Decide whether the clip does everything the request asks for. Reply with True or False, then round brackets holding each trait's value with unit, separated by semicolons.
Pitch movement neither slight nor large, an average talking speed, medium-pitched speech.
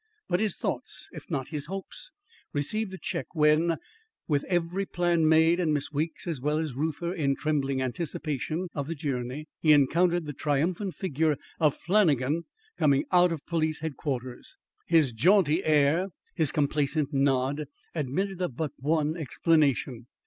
True (3.2 semitones; 150 wpm; 155 Hz)